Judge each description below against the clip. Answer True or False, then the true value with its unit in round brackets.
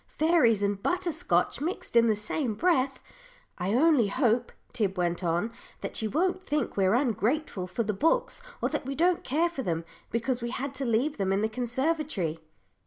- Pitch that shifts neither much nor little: False (7.0 semitones)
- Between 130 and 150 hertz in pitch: False (245 Hz)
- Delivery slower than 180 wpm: False (185 wpm)